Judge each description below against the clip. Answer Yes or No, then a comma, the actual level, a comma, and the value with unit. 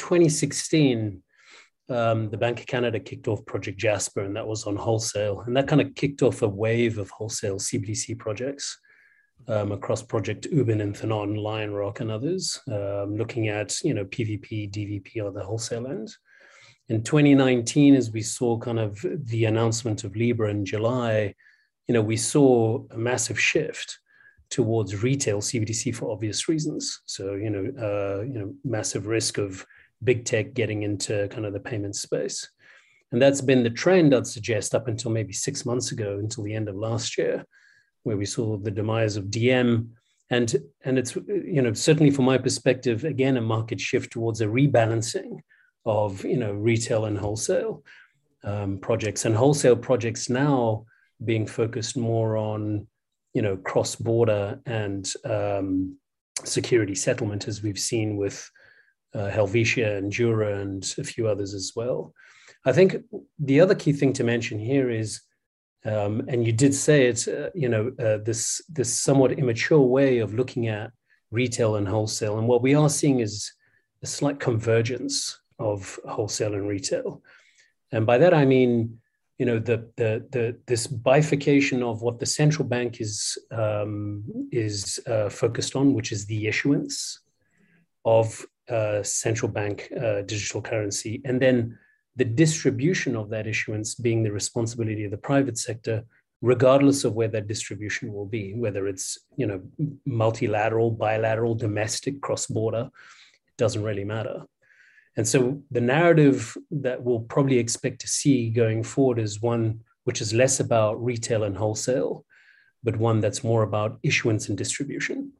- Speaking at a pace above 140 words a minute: Yes, average, 160 wpm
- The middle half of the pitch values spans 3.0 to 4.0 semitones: Yes, average, 3.3 semitones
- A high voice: No, low, 115 Hz